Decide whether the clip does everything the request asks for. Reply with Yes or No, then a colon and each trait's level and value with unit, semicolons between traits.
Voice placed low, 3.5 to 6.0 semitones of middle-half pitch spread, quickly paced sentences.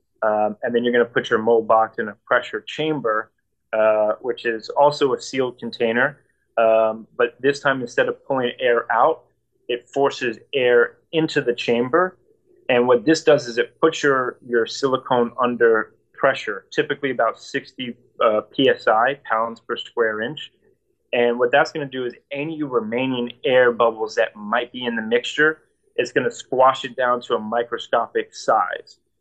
No: low, 125 Hz; average, 4.9 semitones; average, 175 wpm